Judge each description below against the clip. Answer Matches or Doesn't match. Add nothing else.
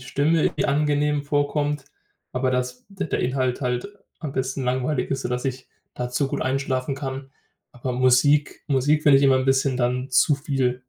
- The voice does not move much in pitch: Matches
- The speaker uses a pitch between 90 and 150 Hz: Matches